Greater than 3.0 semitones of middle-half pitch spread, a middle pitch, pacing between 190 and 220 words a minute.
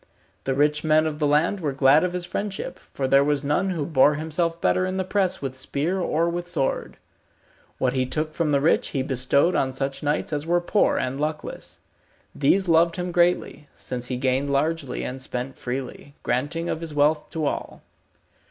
Yes: average, 3.8 semitones; medium, 150 Hz; average, 195 wpm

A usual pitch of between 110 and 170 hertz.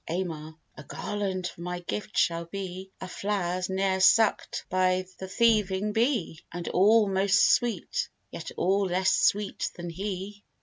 No: high, 190 Hz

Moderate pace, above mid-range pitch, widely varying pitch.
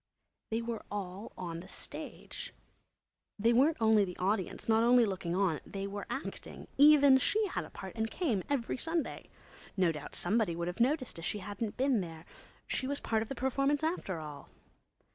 Yes: average, 180 wpm; high, 220 Hz; wide, 6.1 semitones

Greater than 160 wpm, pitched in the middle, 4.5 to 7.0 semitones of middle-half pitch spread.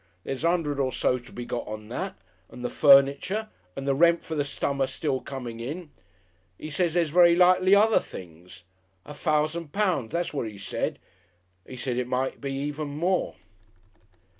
Yes: average, 180 wpm; medium, 145 Hz; average, 5.0 semitones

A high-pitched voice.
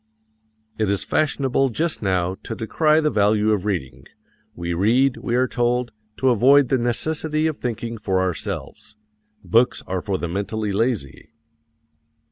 No: low, 115 Hz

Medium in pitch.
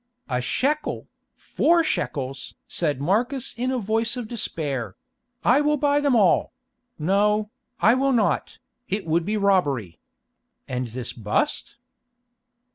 No: high, 210 Hz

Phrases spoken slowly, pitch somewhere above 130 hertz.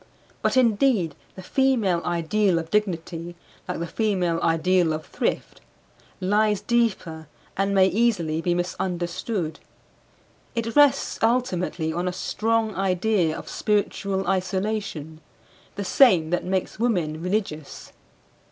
Yes: slow, 115 wpm; medium, 185 Hz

